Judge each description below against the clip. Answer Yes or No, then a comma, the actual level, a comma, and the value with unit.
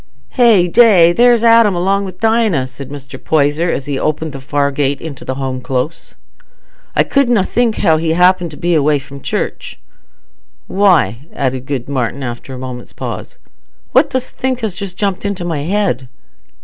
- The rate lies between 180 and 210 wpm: No, average, 165 wpm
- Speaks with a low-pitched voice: No, medium, 160 Hz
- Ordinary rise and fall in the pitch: No, wide, 6.5 semitones